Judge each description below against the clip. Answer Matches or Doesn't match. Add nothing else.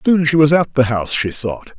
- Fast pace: Matches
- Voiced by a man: Matches